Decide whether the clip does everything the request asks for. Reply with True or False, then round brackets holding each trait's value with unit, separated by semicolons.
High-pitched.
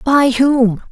True (255 Hz)